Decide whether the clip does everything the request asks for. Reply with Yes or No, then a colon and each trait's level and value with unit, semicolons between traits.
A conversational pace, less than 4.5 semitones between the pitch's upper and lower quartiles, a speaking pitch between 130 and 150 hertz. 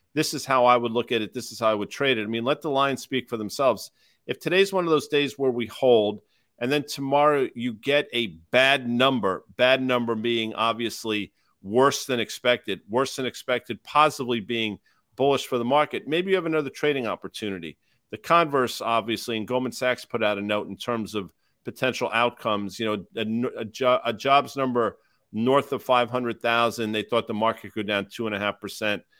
No: average, 195 wpm; average, 3.7 semitones; low, 120 Hz